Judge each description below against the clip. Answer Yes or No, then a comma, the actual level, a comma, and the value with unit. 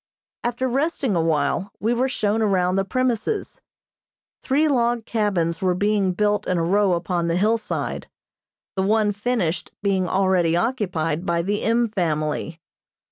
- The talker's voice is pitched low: No, high, 200 Hz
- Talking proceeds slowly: No, average, 145 wpm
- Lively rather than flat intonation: No, average, 4.5 semitones